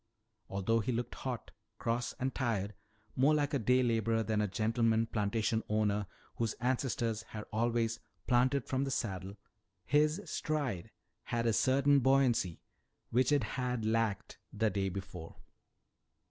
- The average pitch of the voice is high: No, low, 115 Hz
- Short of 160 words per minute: Yes, average, 140 wpm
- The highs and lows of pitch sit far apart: No, average, 3.3 semitones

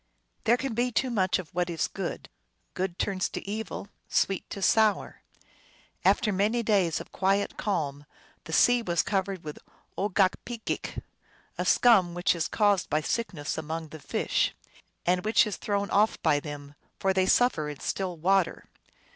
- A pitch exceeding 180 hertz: Yes, high, 190 Hz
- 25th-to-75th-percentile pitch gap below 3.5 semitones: No, average, 4.1 semitones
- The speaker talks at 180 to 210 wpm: No, average, 160 wpm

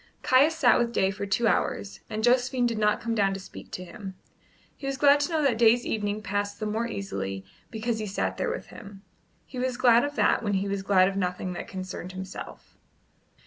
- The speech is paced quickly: Yes, fast, 220 wpm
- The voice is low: No, high, 215 Hz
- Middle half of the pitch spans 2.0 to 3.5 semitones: No, average, 3.9 semitones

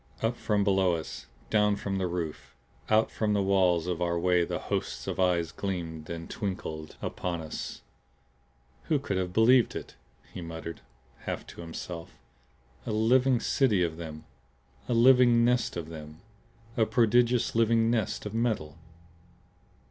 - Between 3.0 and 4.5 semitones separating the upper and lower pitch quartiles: No, average, 5.2 semitones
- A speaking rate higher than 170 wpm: No, average, 150 wpm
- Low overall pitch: Yes, very low, 95 Hz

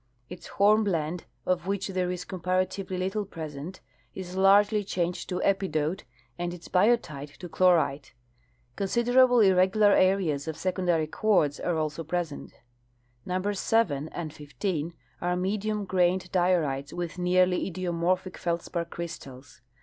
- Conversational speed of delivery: No, slow, 125 wpm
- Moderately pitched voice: Yes, medium, 180 Hz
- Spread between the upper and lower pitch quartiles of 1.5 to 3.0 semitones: Yes, narrow, 2.6 semitones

